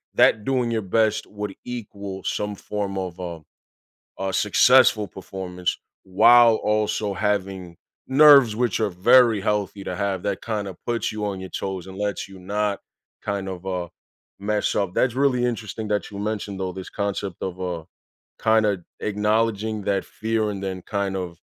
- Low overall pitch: Yes, low, 100 Hz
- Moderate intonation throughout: No, narrow, 2.3 semitones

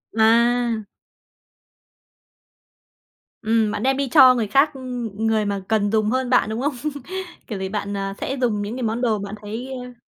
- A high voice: Yes, high, 225 Hz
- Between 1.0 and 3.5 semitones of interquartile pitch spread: Yes, average, 3.0 semitones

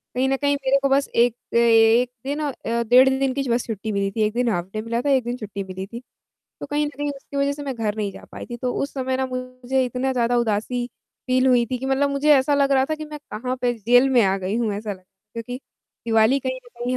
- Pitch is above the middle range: Yes, very high, 250 Hz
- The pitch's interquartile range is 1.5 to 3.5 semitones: Yes, average, 2.8 semitones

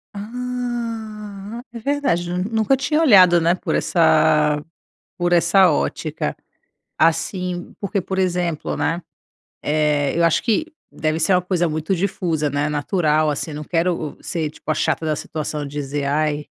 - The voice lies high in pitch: No, medium, 175 Hz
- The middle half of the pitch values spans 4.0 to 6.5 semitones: Yes, average, 4.6 semitones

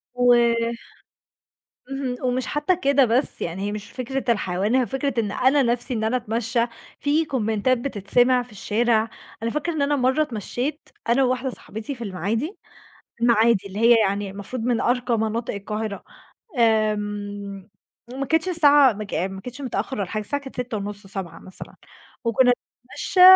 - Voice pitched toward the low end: No, high, 235 Hz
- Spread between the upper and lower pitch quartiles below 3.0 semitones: No, average, 3.9 semitones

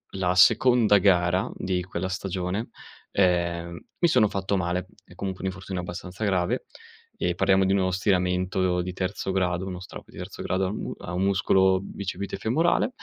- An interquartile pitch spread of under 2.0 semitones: Yes, narrow, 1.4 semitones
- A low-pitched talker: Yes, very low, 95 Hz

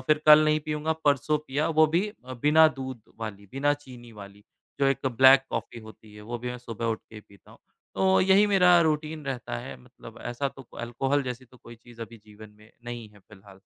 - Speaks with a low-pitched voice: Yes, low, 130 Hz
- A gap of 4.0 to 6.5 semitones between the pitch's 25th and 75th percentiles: Yes, average, 5.0 semitones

